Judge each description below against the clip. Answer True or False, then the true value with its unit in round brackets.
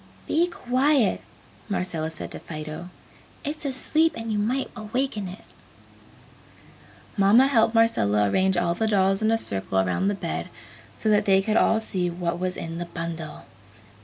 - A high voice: True (195 Hz)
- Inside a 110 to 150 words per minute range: False (160 wpm)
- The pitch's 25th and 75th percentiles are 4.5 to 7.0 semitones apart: True (5.0 semitones)